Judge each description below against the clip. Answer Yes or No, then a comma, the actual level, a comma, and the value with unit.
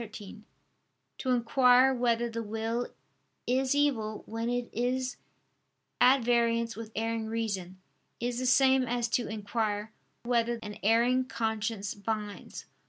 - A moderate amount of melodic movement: No, narrow, 2.1 semitones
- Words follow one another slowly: Yes, slow, 125 wpm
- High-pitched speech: Yes, high, 230 Hz